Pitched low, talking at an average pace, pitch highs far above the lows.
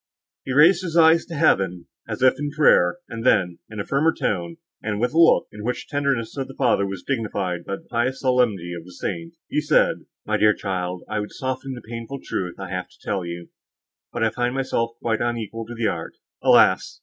No: low, 115 Hz; fast, 220 wpm; wide, 5.7 semitones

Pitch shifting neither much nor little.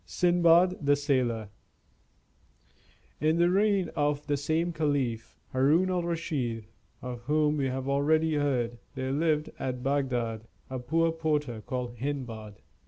Yes: average, 4.3 semitones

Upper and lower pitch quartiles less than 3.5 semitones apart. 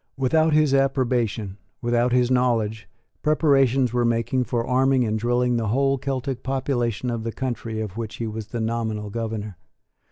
Yes: average, 2.8 semitones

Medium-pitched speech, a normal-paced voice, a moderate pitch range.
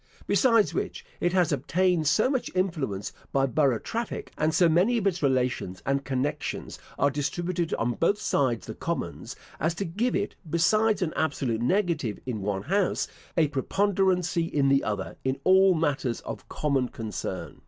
No: medium, 155 Hz; average, 165 wpm; wide, 5.9 semitones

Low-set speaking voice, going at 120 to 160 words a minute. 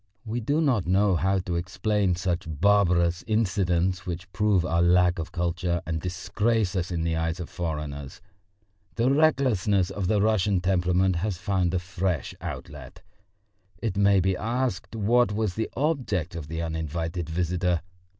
Yes: very low, 90 Hz; average, 155 wpm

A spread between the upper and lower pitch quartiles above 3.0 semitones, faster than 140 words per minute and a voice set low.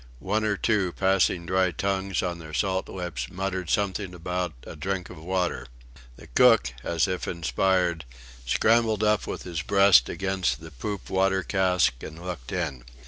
No: narrow, 2.4 semitones; average, 160 wpm; very low, 90 Hz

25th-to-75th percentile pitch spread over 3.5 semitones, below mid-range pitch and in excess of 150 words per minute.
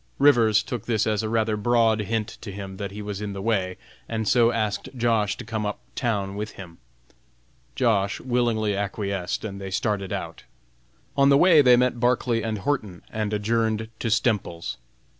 No: narrow, 2.5 semitones; low, 110 Hz; average, 180 wpm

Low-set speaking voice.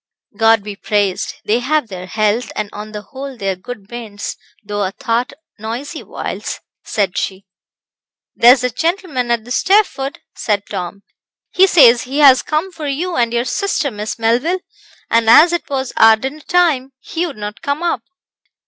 No: high, 240 Hz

